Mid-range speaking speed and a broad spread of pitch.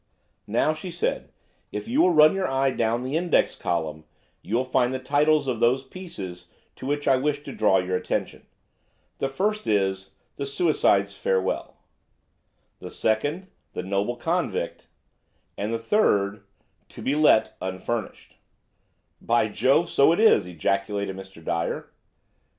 Yes: average, 145 wpm; wide, 7.4 semitones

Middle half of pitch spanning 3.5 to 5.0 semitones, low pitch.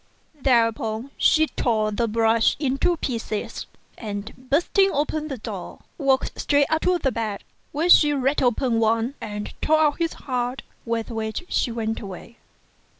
No: average, 4.4 semitones; high, 245 Hz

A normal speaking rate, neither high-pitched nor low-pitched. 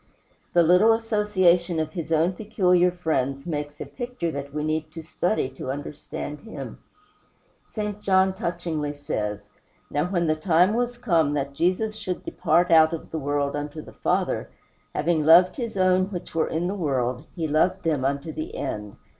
Yes: average, 170 wpm; medium, 165 Hz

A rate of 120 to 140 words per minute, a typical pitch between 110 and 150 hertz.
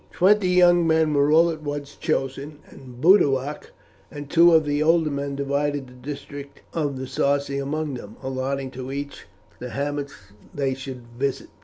No: average, 160 wpm; medium, 140 Hz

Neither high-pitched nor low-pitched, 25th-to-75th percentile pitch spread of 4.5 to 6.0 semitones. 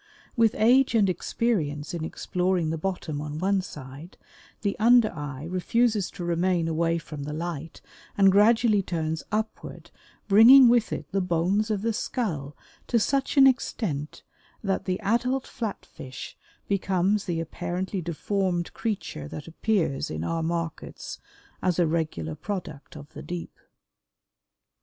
Yes: medium, 180 Hz; average, 4.9 semitones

